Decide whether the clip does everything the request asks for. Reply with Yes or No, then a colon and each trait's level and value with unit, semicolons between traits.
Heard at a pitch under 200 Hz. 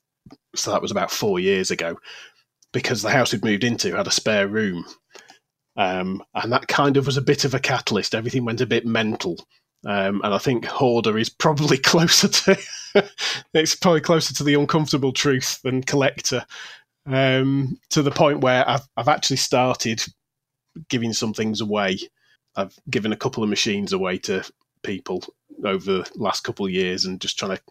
Yes: low, 135 Hz